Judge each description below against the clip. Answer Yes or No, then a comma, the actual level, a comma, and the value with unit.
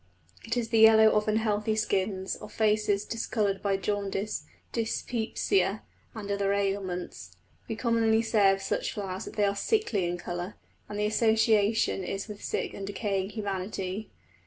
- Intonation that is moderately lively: No, narrow, 2.1 semitones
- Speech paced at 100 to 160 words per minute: Yes, average, 155 wpm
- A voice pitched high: Yes, high, 205 Hz